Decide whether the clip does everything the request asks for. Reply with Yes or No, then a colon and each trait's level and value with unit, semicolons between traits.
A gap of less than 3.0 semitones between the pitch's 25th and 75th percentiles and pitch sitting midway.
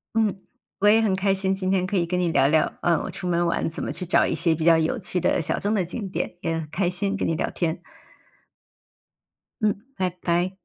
Yes: narrow, 2.6 semitones; medium, 180 Hz